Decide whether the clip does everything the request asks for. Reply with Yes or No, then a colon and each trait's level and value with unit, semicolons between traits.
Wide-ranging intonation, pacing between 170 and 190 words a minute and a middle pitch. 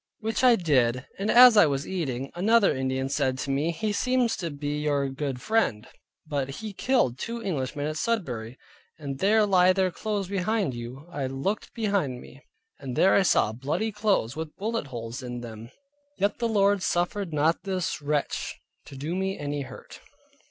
Yes: wide, 7.1 semitones; average, 180 wpm; medium, 155 Hz